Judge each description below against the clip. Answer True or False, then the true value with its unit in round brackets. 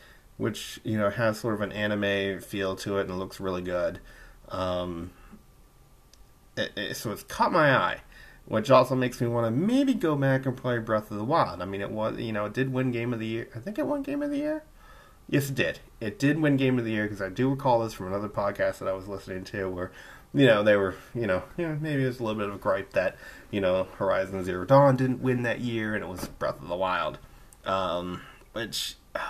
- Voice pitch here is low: True (110 Hz)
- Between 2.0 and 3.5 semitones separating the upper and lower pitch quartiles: False (5.2 semitones)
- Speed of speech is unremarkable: False (245 wpm)